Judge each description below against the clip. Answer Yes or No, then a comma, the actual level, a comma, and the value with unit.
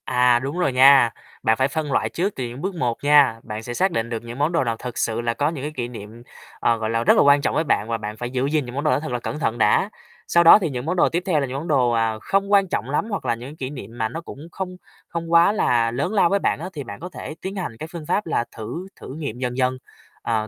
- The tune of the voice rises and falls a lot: Yes, wide, 5.8 semitones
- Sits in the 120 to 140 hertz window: Yes, low, 135 Hz